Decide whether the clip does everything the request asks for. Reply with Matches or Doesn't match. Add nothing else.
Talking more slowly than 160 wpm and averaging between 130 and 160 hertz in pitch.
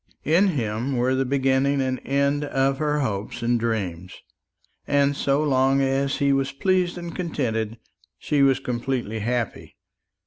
Matches